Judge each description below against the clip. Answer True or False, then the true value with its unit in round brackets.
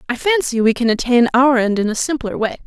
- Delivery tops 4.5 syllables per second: True (5.9 syllables/s)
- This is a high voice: True (250 Hz)